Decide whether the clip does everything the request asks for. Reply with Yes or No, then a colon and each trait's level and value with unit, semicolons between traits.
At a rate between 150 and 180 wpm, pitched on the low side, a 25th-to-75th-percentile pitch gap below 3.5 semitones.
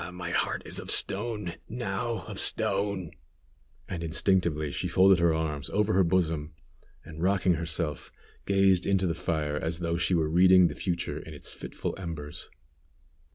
Yes: average, 160 wpm; very low, 90 Hz; average, 3.0 semitones